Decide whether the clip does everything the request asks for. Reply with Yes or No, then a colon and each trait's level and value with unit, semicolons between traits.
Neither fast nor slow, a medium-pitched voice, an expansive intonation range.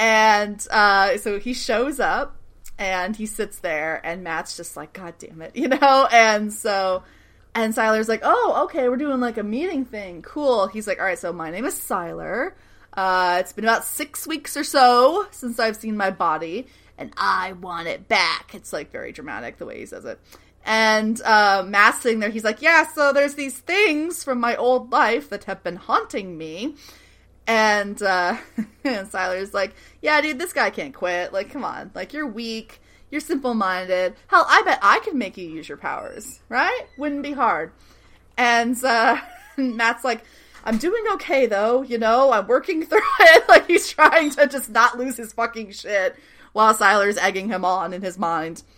No: average, 195 wpm; high, 225 Hz; wide, 6.2 semitones